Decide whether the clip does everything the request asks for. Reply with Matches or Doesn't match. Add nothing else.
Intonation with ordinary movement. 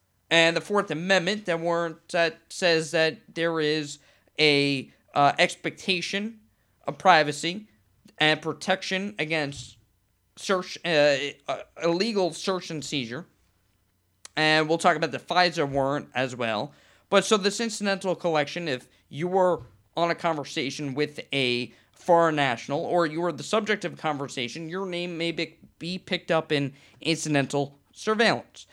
Matches